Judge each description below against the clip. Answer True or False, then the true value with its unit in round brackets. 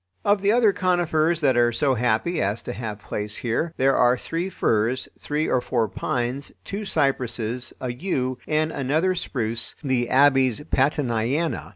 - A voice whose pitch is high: False (130 Hz)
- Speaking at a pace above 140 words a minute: True (160 wpm)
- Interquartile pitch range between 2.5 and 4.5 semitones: False (5.0 semitones)